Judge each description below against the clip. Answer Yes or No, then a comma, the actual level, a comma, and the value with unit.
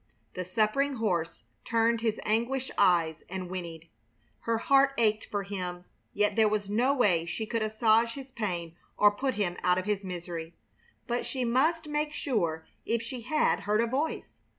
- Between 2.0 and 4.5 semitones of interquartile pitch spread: No, average, 5.0 semitones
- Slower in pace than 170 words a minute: No, average, 175 wpm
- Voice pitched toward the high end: Yes, high, 215 Hz